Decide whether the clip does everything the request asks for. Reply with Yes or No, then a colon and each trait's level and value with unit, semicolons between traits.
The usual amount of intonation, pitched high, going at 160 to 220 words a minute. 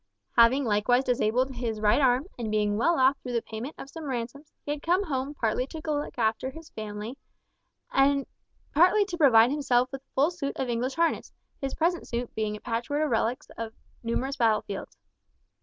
Yes: average, 4.0 semitones; very high, 255 Hz; average, 190 wpm